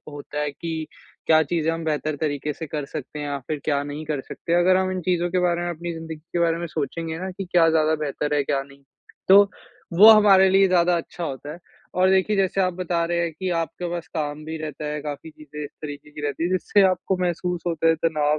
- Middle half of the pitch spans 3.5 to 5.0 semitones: No, average, 2.9 semitones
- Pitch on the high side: No, medium, 165 Hz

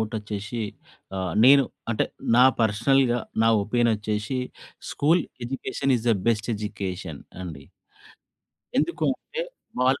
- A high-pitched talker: No, low, 110 Hz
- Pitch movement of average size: Yes, average, 4.3 semitones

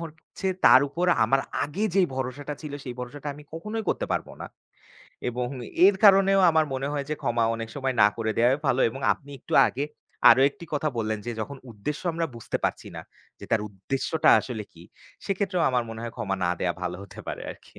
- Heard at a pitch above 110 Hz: Yes, low, 135 Hz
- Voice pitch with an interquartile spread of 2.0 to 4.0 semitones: No, wide, 5.6 semitones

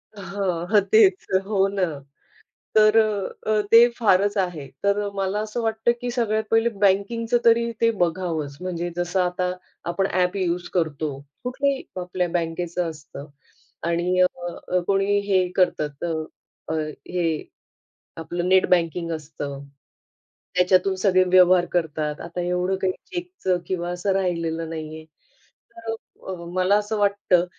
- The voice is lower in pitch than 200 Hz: Yes, medium, 185 Hz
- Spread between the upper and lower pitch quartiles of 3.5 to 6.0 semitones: No, average, 2.9 semitones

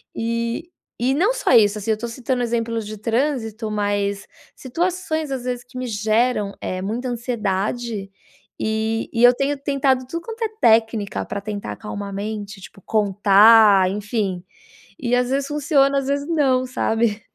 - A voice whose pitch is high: Yes, high, 230 Hz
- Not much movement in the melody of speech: No, average, 3.9 semitones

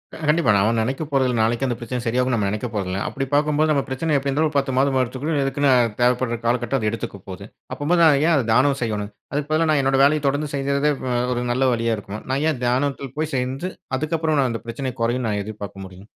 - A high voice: No, low, 130 Hz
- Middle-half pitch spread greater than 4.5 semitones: No, average, 3.7 semitones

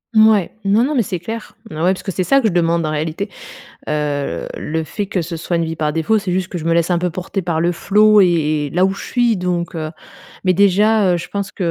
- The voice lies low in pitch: No, medium, 180 Hz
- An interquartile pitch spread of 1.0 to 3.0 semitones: No, average, 3.6 semitones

